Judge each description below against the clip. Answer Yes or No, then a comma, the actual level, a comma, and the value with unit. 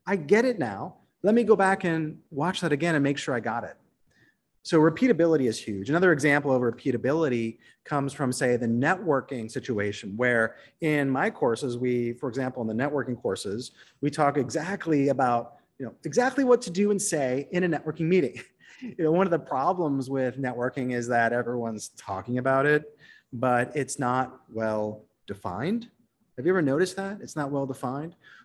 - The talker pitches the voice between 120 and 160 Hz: Yes, medium, 140 Hz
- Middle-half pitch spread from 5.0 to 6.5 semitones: Yes, wide, 5.4 semitones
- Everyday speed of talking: Yes, average, 185 wpm